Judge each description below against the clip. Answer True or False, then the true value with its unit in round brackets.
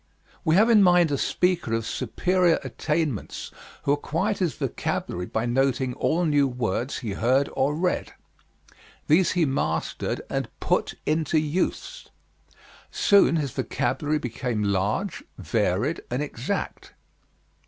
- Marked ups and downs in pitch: True (5.9 semitones)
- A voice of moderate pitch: True (145 Hz)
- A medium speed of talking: False (125 wpm)